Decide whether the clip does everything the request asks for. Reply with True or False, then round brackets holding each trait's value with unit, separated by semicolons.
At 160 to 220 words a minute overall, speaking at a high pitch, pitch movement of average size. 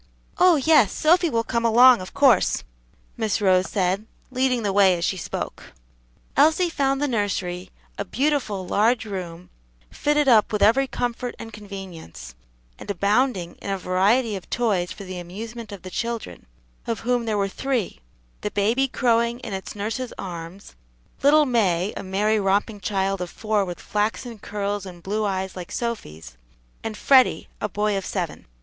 True (165 wpm; 210 Hz; 4.1 semitones)